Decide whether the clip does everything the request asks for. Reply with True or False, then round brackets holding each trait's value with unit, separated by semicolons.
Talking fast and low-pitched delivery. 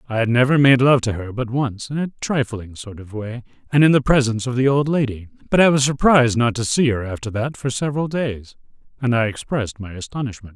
True (235 wpm; 125 Hz)